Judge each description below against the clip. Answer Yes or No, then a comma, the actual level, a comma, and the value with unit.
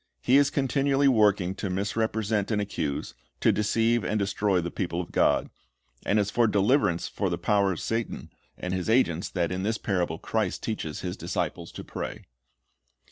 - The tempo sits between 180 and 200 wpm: Yes, average, 185 wpm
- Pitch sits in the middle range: No, low, 105 Hz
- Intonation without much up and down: No, average, 3.6 semitones